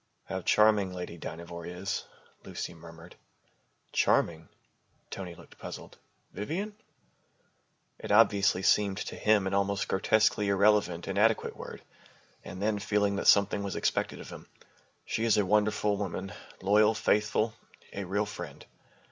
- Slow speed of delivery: Yes, slow, 130 wpm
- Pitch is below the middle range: Yes, low, 100 Hz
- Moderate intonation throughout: No, narrow, 2.2 semitones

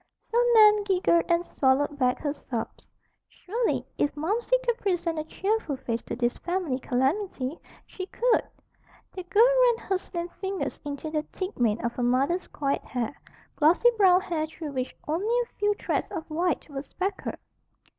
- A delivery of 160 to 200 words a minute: Yes, average, 165 wpm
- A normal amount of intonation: No, wide, 6.2 semitones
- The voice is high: Yes, very high, 340 Hz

